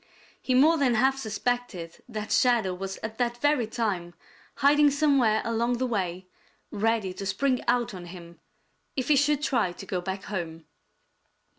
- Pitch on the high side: Yes, high, 230 Hz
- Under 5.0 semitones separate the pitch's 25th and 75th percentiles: No, wide, 5.5 semitones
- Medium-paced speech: Yes, average, 160 wpm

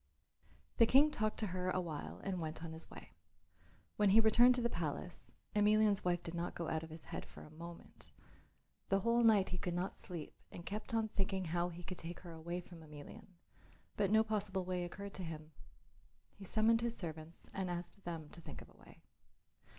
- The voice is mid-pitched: Yes, medium, 180 Hz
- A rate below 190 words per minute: No, fast, 205 wpm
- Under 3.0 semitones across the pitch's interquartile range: No, average, 3.8 semitones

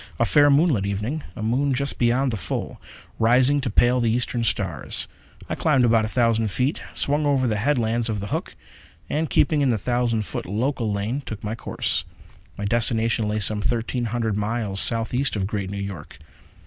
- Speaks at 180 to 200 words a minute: Yes, average, 185 wpm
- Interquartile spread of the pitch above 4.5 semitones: No, average, 3.5 semitones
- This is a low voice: Yes, low, 115 Hz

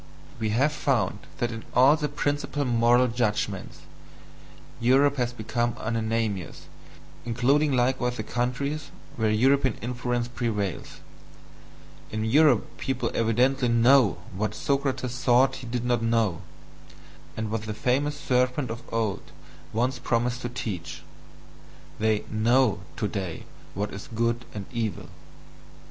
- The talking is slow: Yes, slow, 125 wpm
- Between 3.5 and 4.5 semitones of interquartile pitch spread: No, average, 2.7 semitones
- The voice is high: No, low, 120 Hz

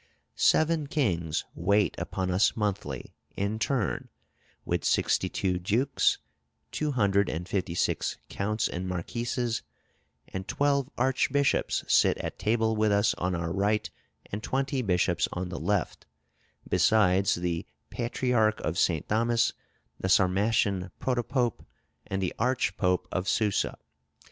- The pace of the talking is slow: Yes, slow, 125 wpm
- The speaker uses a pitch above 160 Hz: No, low, 105 Hz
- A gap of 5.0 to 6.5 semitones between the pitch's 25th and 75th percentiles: No, average, 4.5 semitones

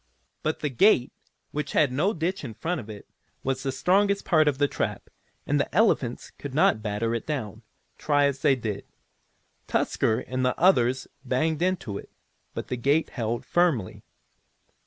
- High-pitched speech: No, low, 135 Hz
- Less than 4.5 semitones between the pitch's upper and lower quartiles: No, average, 5.3 semitones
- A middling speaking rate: Yes, average, 170 wpm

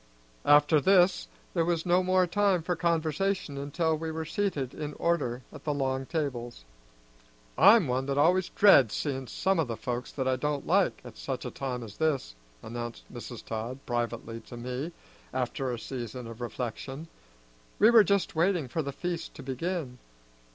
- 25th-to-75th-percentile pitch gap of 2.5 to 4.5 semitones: No, wide, 5.4 semitones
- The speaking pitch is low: No, medium, 145 Hz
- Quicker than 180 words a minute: No, average, 170 wpm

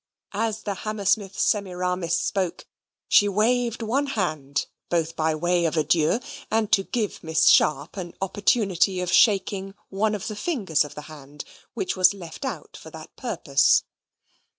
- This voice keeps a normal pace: Yes, average, 150 wpm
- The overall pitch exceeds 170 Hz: Yes, high, 190 Hz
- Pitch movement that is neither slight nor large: Yes, average, 4.3 semitones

